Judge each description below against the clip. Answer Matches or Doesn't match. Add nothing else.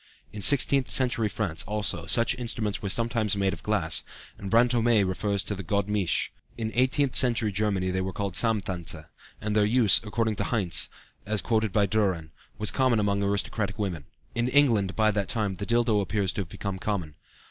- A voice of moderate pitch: Doesn't match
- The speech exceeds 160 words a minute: Matches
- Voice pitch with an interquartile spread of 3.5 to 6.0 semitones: Doesn't match